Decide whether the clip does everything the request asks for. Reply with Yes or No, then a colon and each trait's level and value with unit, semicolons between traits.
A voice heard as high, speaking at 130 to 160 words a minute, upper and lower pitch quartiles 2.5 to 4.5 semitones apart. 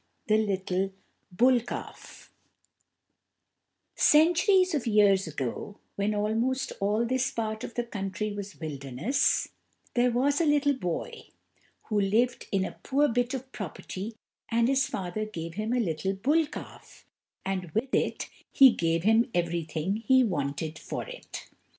No: high, 215 Hz; average, 140 wpm; average, 5.2 semitones